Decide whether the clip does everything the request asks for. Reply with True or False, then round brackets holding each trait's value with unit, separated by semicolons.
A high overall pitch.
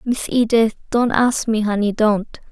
True (225 Hz)